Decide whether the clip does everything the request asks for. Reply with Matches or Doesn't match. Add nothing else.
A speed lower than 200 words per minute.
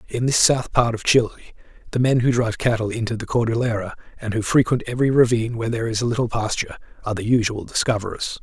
Doesn't match